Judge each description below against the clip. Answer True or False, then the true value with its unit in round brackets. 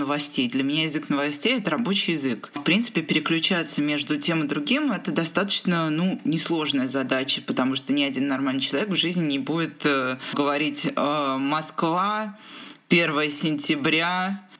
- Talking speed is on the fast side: False (150 wpm)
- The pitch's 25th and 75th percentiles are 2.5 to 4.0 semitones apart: False (4.4 semitones)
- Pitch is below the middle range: False (160 Hz)